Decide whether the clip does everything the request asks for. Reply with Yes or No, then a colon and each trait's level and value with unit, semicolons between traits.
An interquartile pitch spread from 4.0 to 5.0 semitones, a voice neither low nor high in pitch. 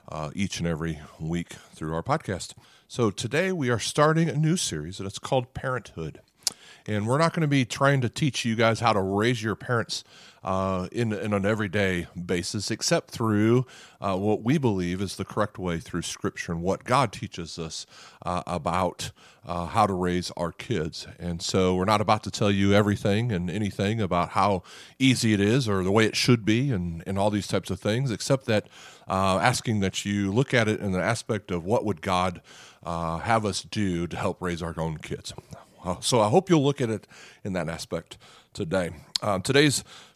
No: average, 4.7 semitones; low, 105 Hz